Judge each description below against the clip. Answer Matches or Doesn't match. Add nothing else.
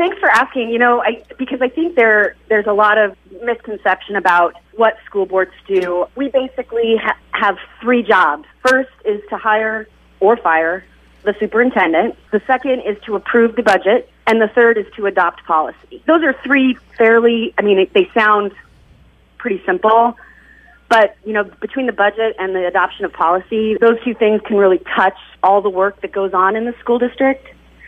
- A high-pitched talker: Matches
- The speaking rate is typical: Matches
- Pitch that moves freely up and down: Doesn't match